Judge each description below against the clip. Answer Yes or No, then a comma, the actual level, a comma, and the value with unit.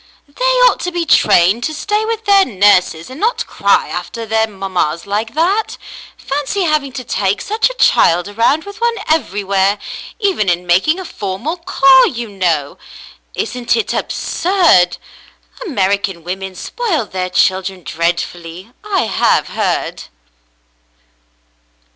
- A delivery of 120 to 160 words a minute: Yes, slow, 135 wpm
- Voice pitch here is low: No, high, 225 Hz